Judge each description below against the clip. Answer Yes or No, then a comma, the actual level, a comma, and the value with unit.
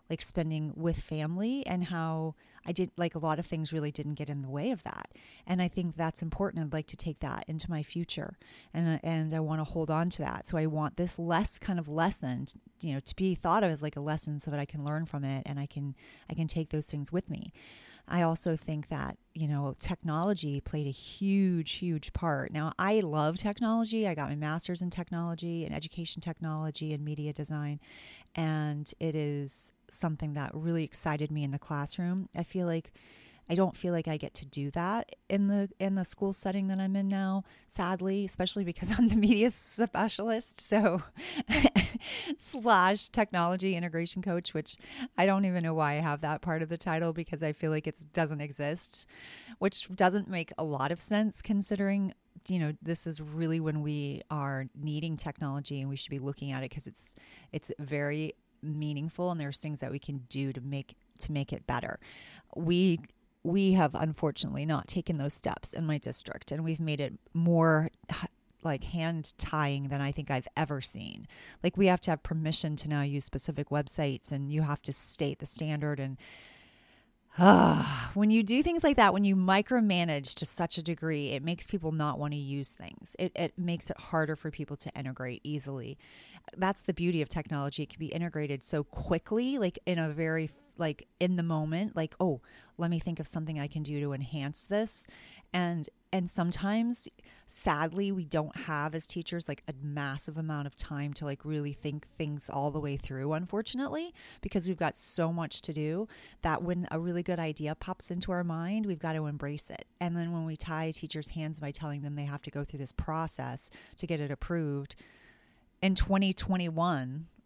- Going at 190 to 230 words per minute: Yes, average, 200 wpm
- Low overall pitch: No, medium, 160 Hz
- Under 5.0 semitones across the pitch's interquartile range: Yes, average, 3.4 semitones